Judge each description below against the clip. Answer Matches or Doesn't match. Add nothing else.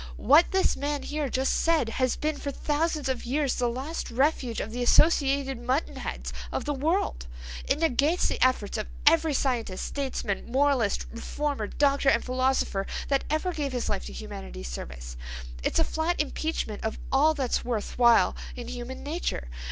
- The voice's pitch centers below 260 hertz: Doesn't match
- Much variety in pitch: Doesn't match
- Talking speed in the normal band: Matches